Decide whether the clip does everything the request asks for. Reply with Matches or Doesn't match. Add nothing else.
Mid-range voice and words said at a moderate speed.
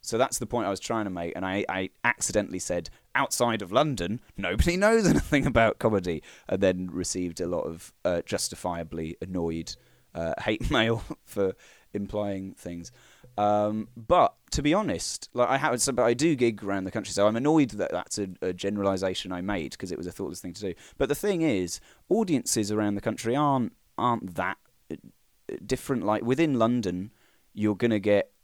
Doesn't match